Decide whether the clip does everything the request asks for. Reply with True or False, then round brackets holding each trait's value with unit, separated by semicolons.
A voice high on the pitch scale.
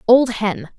True (230 Hz)